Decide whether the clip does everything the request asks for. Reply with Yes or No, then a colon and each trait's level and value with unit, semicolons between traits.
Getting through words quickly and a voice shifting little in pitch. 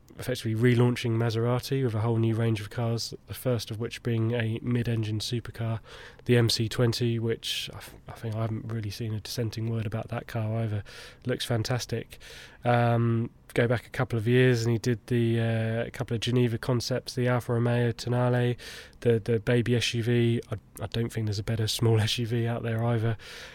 No: average, 190 wpm; narrow, 1.2 semitones